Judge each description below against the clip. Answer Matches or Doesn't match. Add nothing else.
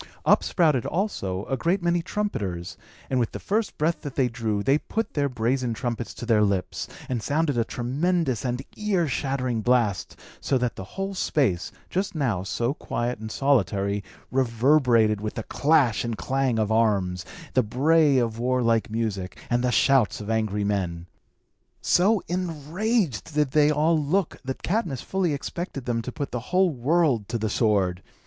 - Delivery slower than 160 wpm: Doesn't match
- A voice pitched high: Doesn't match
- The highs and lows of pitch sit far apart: Matches